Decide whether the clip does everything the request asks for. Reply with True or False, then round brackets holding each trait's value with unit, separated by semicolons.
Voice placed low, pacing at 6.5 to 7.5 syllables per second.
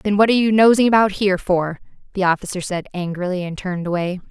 False (190 Hz; 6.6 syllables/s)